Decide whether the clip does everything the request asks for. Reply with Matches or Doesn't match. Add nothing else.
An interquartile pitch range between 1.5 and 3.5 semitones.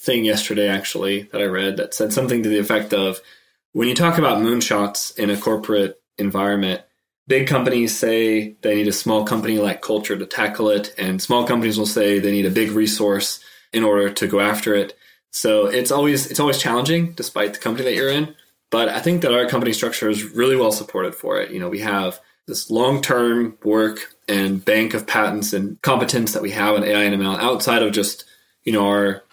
Matches